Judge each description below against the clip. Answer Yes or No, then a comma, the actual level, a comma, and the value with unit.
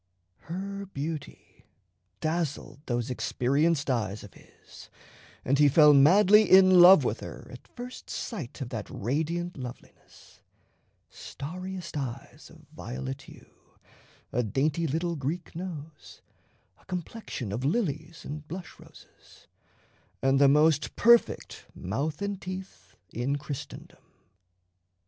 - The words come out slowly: Yes, slow, 115 wpm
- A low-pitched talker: No, medium, 155 Hz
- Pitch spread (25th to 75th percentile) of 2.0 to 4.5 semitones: No, average, 5.1 semitones